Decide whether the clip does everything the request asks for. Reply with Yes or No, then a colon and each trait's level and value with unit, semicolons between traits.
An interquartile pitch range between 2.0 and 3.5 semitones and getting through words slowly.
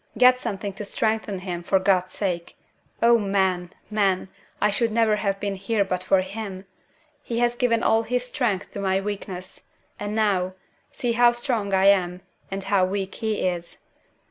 No: average, 2.9 semitones; average, 170 wpm